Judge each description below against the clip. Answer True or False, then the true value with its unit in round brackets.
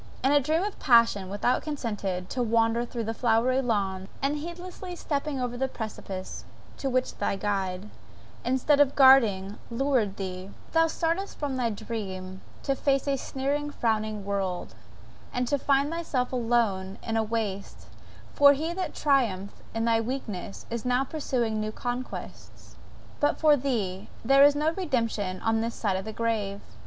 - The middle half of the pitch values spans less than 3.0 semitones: False (5.1 semitones)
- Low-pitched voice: False (235 Hz)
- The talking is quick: False (160 wpm)